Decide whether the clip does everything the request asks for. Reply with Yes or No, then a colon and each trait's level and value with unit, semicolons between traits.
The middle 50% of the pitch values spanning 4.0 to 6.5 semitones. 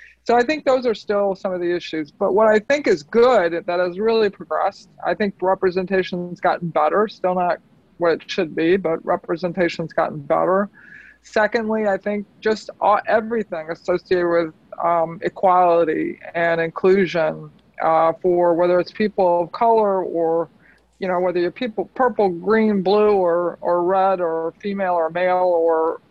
No: average, 3.5 semitones